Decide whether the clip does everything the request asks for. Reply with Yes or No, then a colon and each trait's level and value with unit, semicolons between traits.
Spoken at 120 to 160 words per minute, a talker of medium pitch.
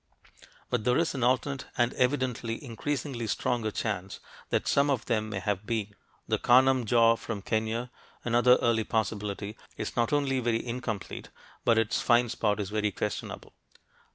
No: average, 155 wpm; low, 115 Hz